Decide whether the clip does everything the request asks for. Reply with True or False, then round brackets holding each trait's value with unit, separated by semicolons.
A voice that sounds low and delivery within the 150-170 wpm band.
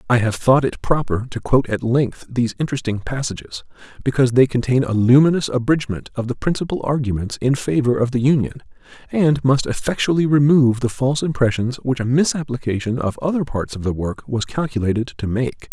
False (130 Hz; 180 wpm)